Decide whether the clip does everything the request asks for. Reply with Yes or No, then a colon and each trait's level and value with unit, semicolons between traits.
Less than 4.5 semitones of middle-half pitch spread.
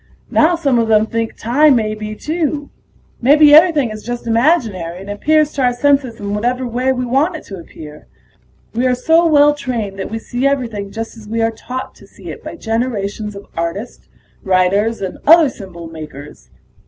No: average, 5.3 semitones